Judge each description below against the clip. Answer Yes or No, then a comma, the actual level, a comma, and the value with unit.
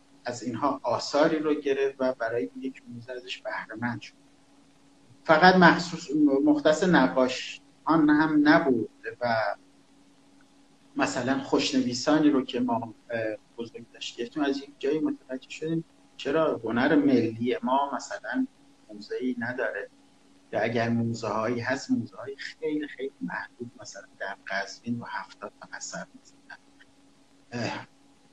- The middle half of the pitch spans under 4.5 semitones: No, average, 4.8 semitones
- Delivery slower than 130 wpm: Yes, average, 120 wpm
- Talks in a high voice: No, medium, 140 Hz